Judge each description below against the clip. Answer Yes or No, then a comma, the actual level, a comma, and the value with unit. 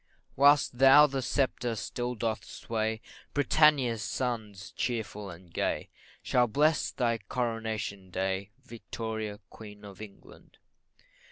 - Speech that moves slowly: Yes, slow, 110 wpm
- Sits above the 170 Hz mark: No, low, 115 Hz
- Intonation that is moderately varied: Yes, average, 3.3 semitones